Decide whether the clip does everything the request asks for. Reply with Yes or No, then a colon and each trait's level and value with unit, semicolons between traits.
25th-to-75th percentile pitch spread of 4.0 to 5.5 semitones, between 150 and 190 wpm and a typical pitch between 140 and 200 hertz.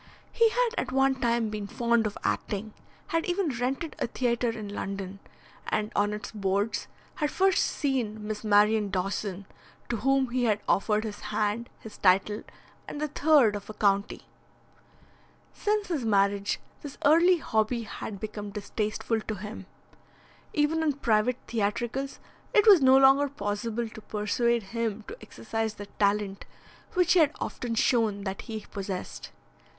No: average, 4.5 semitones; average, 155 wpm; high, 220 Hz